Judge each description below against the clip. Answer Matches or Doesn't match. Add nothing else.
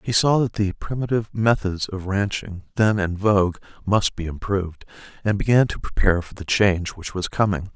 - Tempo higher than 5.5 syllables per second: Doesn't match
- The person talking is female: Doesn't match